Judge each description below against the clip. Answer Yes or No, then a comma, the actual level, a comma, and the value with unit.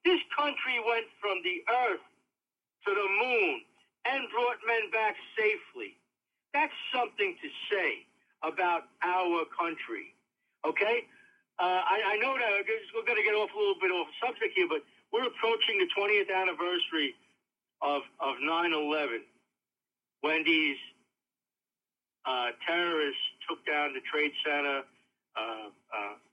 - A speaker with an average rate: No, slow, 130 wpm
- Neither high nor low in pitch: No, high, 205 Hz